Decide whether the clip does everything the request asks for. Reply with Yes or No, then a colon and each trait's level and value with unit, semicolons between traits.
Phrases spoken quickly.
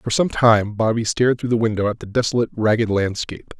Yes: fast, 215 wpm